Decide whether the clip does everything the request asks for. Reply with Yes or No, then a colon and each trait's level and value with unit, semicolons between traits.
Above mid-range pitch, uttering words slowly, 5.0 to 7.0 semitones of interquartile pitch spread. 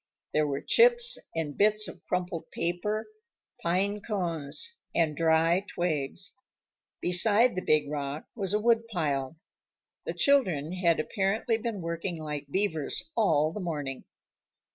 No: medium, 175 Hz; slow, 125 wpm; average, 5.3 semitones